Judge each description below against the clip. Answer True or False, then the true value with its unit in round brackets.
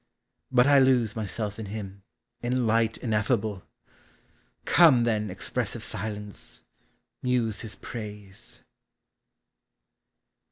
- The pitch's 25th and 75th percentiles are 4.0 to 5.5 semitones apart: False (2.9 semitones)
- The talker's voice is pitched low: True (110 Hz)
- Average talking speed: False (90 wpm)